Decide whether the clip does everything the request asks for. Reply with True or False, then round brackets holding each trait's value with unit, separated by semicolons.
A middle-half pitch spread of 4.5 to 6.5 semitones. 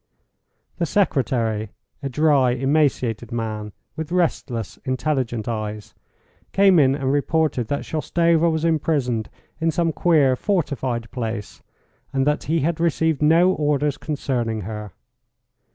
True (5.3 semitones)